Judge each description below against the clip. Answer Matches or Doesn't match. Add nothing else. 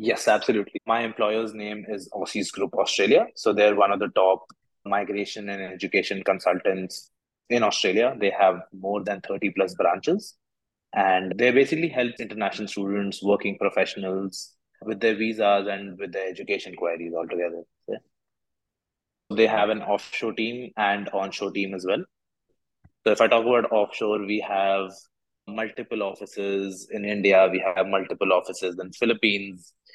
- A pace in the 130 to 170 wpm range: Matches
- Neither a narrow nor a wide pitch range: Doesn't match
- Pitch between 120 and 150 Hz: Doesn't match